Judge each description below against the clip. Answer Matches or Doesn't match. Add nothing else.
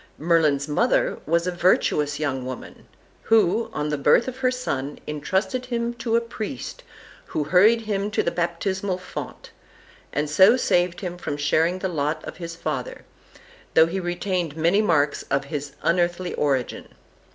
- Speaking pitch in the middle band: Matches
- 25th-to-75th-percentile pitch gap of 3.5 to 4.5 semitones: Doesn't match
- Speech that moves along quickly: Doesn't match